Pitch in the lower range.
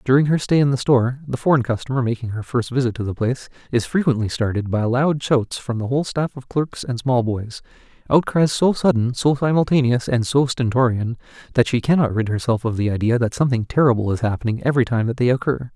Yes: low, 125 Hz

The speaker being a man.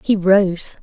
No: female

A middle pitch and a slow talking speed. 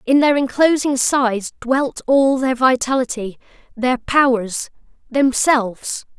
No: very high, 255 Hz; slow, 85 wpm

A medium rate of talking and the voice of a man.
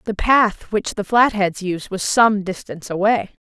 No: average, 175 wpm; female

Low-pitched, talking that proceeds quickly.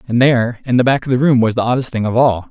Yes: low, 120 Hz; fast, 335 wpm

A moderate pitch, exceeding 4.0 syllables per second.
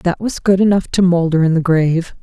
Yes: medium, 175 Hz; 5.6 syllables/s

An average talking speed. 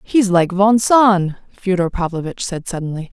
Yes: average, 150 wpm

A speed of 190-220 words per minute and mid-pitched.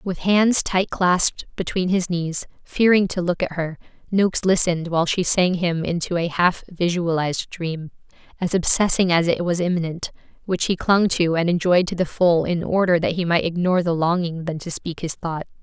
Yes: average, 195 wpm; medium, 175 Hz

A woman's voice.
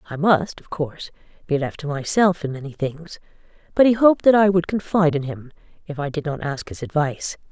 Yes: female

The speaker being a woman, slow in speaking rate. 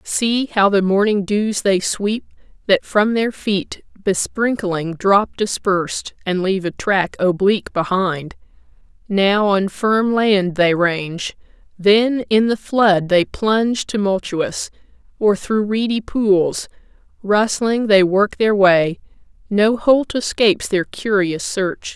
Yes: female; slow, 130 wpm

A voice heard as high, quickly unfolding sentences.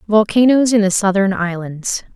No: high, 205 Hz; average, 140 wpm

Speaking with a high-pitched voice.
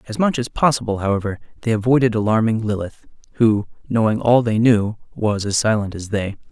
No: low, 110 Hz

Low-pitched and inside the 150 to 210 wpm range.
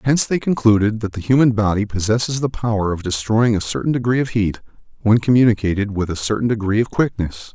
Yes: low, 110 Hz; average, 200 wpm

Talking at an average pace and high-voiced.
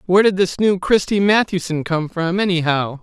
No: average, 180 wpm; medium, 180 Hz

